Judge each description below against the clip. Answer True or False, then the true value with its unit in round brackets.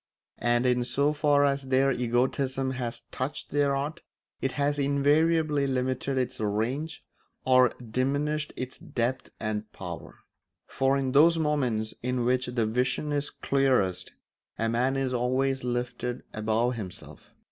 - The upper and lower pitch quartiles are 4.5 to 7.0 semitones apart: False (2.5 semitones)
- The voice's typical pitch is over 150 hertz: False (130 Hz)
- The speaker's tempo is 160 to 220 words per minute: False (135 wpm)